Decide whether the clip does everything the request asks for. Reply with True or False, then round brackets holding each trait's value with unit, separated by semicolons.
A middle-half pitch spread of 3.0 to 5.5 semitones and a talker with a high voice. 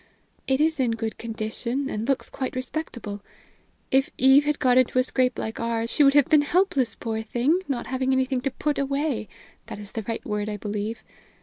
True (3.5 semitones; 255 Hz)